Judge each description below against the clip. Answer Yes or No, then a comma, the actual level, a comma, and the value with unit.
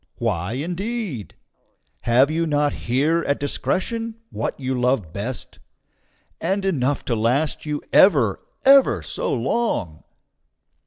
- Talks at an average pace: No, slow, 115 wpm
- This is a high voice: No, medium, 140 Hz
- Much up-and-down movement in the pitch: Yes, wide, 6.6 semitones